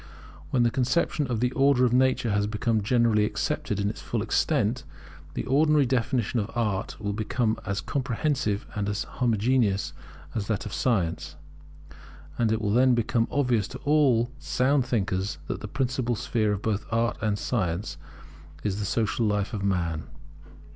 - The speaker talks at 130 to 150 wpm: No, average, 165 wpm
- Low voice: Yes, low, 115 Hz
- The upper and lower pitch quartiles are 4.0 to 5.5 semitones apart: No, average, 3.6 semitones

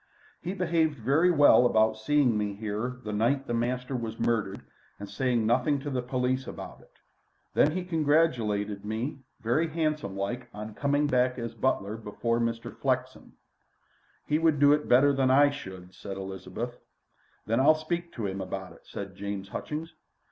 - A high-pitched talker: No, low, 125 Hz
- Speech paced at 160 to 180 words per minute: Yes, average, 170 wpm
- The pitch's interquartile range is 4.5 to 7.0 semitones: Yes, average, 5.2 semitones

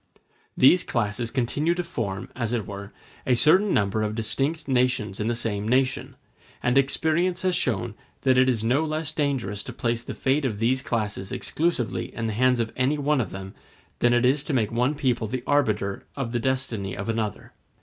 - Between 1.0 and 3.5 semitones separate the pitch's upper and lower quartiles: No, average, 4.1 semitones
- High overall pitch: No, low, 120 Hz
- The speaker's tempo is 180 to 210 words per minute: Yes, average, 195 wpm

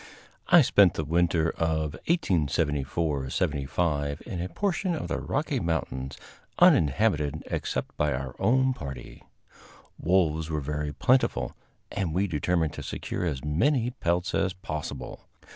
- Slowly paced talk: Yes, slow, 130 wpm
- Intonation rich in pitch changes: No, average, 4.7 semitones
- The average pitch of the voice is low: Yes, very low, 80 Hz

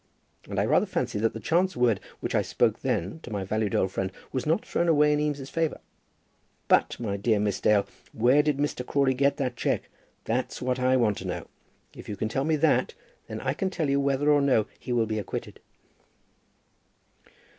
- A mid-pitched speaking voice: No, low, 130 Hz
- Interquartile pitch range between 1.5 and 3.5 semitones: No, average, 5.1 semitones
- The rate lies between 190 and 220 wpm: Yes, fast, 205 wpm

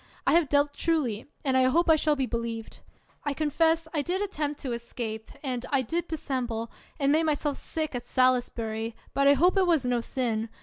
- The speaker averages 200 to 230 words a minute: Yes, fast, 205 wpm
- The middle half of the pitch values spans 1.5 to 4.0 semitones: No, average, 4.7 semitones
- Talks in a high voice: Yes, very high, 275 Hz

